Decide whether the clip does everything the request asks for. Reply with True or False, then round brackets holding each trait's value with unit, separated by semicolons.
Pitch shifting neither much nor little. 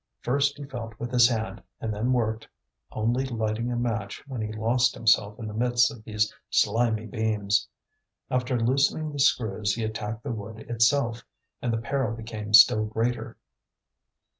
False (2.2 semitones)